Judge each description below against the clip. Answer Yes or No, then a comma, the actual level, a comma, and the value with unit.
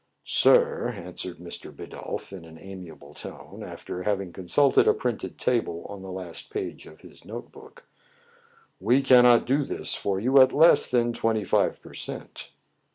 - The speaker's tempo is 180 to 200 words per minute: No, average, 165 wpm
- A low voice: Yes, low, 115 Hz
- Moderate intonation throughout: No, wide, 6.8 semitones